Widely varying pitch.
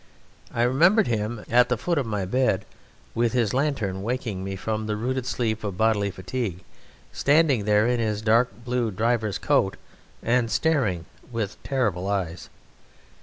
No: average, 3.6 semitones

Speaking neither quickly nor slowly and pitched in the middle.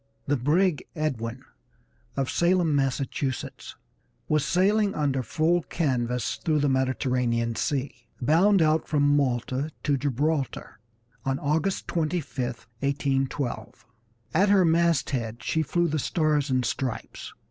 No: slow, 120 wpm; medium, 145 Hz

